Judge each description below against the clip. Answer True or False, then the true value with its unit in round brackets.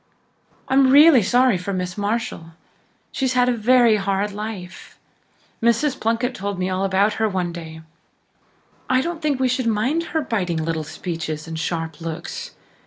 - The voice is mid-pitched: False (210 Hz)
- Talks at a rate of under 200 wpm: True (160 wpm)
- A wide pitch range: True (6.0 semitones)